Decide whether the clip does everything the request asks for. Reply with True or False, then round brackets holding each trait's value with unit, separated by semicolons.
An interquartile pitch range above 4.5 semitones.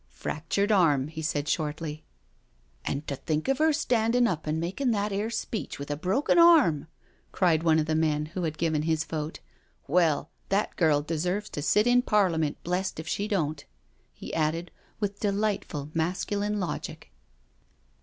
True (5.1 semitones)